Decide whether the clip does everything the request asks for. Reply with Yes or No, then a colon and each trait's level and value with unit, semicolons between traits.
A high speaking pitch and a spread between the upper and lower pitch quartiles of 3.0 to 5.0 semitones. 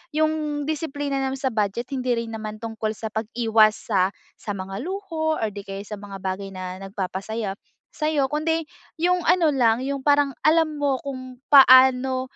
No: very high, 255 Hz; wide, 5.5 semitones